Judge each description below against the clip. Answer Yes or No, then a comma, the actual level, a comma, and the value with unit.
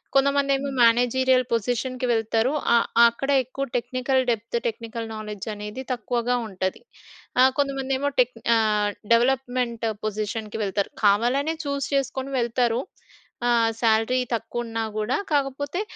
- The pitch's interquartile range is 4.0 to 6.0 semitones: No, average, 2.9 semitones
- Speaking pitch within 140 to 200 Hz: No, high, 240 Hz